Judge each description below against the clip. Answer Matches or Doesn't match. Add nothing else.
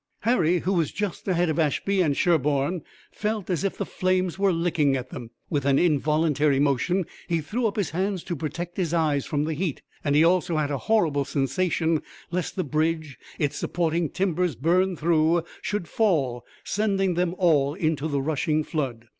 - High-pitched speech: Doesn't match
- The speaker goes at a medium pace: Matches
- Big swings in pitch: Doesn't match